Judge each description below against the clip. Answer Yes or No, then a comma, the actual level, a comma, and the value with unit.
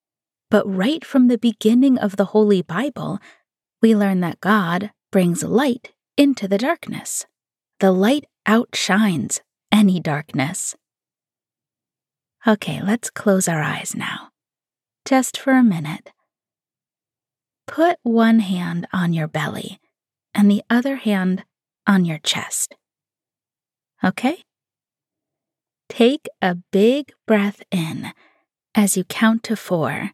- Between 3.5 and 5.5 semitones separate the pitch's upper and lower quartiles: Yes, average, 4.0 semitones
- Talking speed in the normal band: No, slow, 115 wpm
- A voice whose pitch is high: Yes, high, 210 Hz